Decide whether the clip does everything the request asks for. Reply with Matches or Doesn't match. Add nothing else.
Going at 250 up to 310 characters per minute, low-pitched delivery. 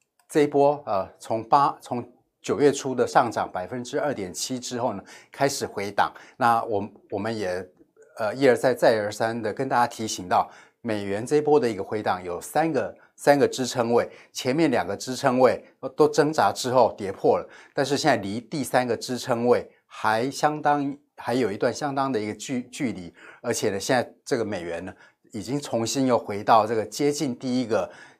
Matches